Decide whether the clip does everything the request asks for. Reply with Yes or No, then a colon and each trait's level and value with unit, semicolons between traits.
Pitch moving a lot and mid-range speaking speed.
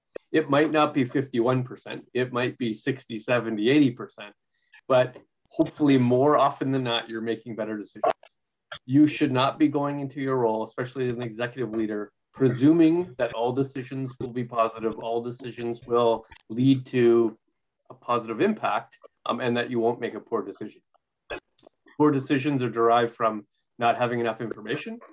No: average, 2.8 semitones; average, 160 wpm